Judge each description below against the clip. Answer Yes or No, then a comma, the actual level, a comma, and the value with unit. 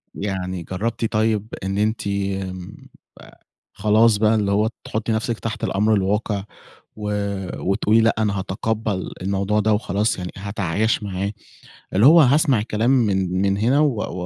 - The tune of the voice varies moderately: No, narrow, 2.3 semitones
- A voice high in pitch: No, low, 105 Hz